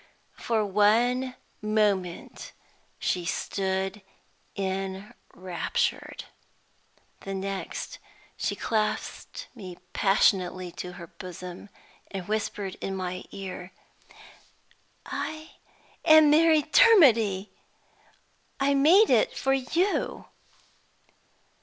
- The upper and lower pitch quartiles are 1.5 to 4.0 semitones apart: No, wide, 5.6 semitones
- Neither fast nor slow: No, slow, 80 wpm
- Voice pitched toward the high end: Yes, high, 205 Hz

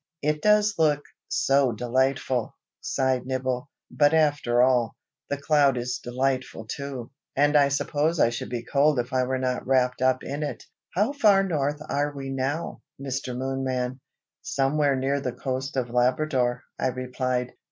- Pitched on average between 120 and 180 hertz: Yes, low, 135 Hz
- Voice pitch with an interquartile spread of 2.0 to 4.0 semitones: Yes, narrow, 2.4 semitones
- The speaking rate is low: No, average, 155 wpm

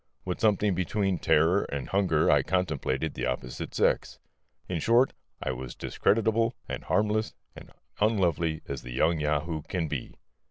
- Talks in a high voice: No, very low, 85 Hz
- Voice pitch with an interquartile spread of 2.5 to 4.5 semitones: No, wide, 5.4 semitones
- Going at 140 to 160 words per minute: Yes, average, 150 wpm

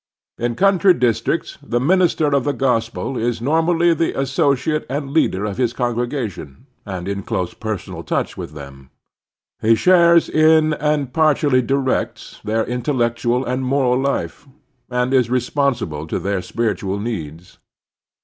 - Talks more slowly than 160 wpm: Yes, average, 150 wpm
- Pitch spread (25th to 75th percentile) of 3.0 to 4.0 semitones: No, average, 4.8 semitones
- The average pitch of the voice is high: No, low, 125 Hz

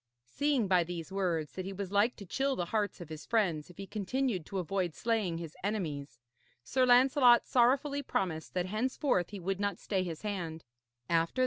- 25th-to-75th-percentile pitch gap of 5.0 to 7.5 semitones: Yes, average, 5.3 semitones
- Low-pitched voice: No, high, 195 Hz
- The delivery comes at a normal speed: Yes, average, 185 wpm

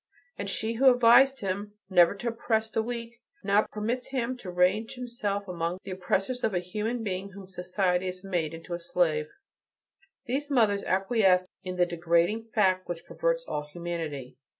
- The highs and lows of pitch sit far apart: No, average, 4.3 semitones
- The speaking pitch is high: Yes, high, 195 Hz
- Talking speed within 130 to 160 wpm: No, average, 170 wpm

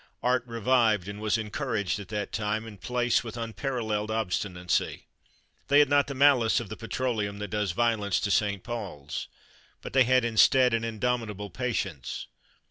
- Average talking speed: Yes, average, 160 wpm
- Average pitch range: Yes, average, 3.2 semitones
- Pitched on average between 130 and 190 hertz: No, low, 110 Hz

